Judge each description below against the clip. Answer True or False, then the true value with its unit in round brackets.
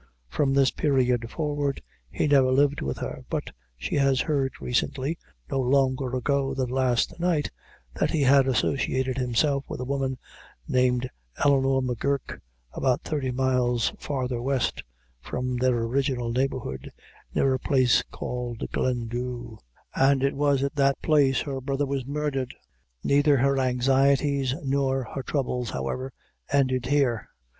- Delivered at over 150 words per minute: False (140 wpm)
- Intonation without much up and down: True (1.8 semitones)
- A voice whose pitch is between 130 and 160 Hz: True (135 Hz)